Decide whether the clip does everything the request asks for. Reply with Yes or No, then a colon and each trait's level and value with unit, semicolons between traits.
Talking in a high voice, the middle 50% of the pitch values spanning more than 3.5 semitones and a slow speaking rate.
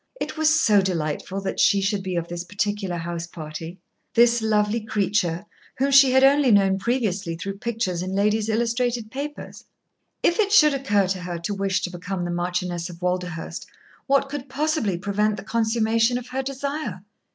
No: high, 205 Hz; average, 5.2 semitones; average, 175 wpm